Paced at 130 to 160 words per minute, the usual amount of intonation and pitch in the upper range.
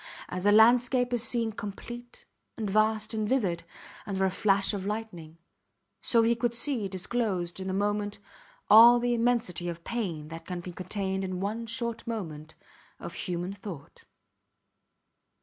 Yes: average, 150 wpm; average, 4.1 semitones; high, 205 Hz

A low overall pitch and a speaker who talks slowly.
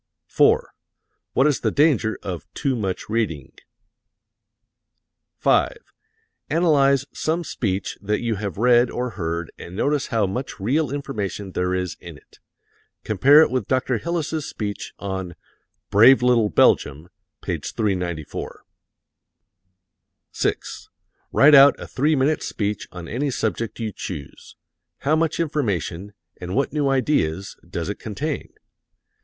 Yes: low, 115 Hz; slow, 130 wpm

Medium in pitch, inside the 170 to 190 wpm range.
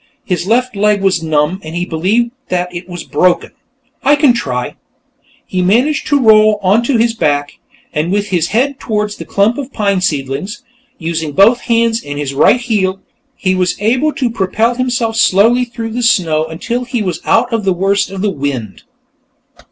No: high, 200 Hz; average, 175 wpm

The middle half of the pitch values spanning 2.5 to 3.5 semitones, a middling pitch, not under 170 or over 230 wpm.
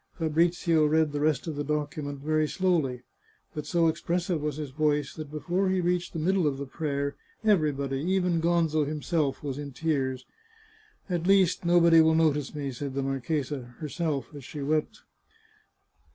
Yes: average, 3.1 semitones; medium, 155 Hz; average, 175 wpm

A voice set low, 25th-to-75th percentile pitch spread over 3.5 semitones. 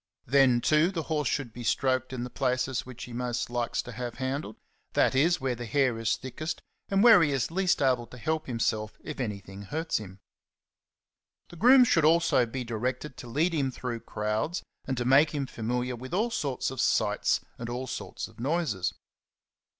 Yes: low, 130 Hz; average, 4.2 semitones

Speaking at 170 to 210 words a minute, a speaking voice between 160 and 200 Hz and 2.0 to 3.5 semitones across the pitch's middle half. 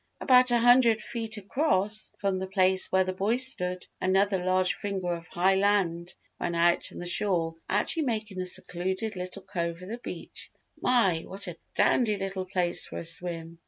Yes: average, 180 wpm; high, 190 Hz; average, 3.0 semitones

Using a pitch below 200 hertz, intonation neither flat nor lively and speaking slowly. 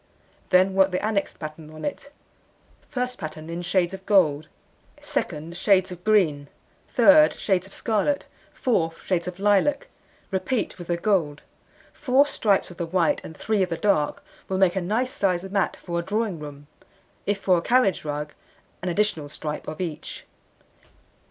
No: medium, 185 Hz; average, 4.0 semitones; average, 165 wpm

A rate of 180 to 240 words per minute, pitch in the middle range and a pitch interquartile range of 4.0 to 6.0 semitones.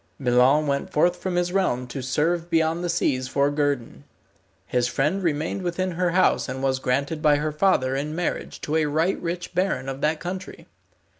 Yes: average, 190 wpm; medium, 155 Hz; average, 4.4 semitones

